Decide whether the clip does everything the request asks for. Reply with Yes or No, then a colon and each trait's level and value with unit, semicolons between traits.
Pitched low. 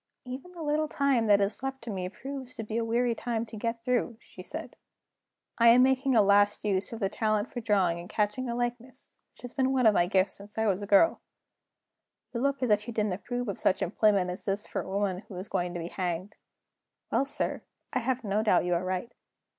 No: high, 220 Hz